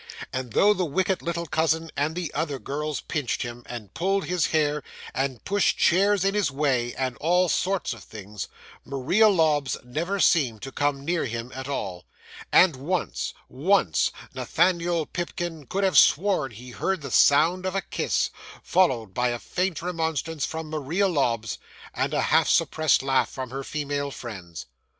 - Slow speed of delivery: No, average, 165 wpm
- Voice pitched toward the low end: No, medium, 150 Hz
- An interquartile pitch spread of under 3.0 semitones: No, wide, 5.4 semitones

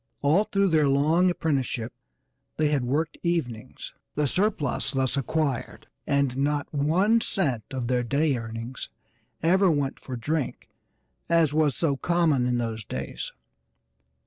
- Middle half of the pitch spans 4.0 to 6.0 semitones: Yes, average, 4.4 semitones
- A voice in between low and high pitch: Yes, medium, 145 Hz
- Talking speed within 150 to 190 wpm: No, slow, 135 wpm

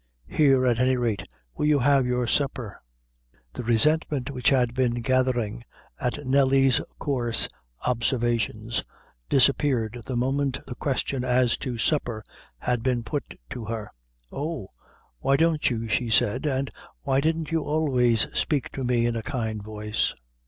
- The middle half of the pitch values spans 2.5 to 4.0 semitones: Yes, average, 2.8 semitones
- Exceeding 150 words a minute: No, average, 145 wpm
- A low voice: Yes, low, 125 Hz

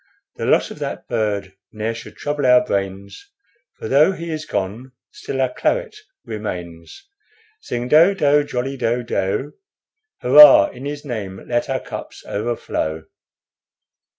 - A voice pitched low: Yes, low, 125 Hz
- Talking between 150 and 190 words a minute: No, average, 140 wpm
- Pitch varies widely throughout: Yes, wide, 5.9 semitones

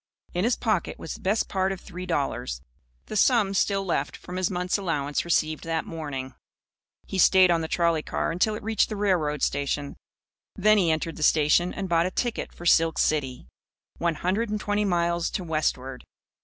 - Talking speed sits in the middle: Yes, average, 190 wpm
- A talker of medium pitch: Yes, medium, 175 Hz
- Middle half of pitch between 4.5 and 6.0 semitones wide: No, average, 3.8 semitones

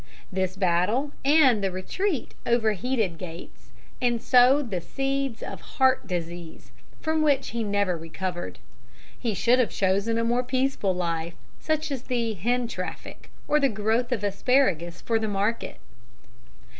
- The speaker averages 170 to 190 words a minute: No, average, 145 wpm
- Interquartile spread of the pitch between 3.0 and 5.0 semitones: No, wide, 5.6 semitones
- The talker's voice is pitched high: Yes, high, 225 Hz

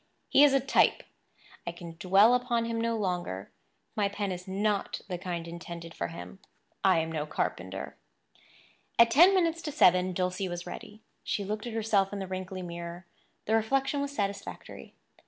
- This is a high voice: Yes, high, 195 Hz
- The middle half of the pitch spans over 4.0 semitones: Yes, average, 4.5 semitones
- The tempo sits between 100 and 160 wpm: No, average, 175 wpm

